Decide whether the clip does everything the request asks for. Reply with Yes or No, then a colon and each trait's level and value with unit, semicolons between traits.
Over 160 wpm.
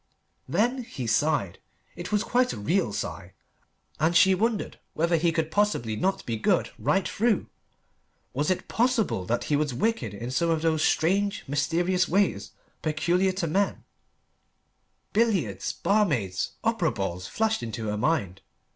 No: average, 145 wpm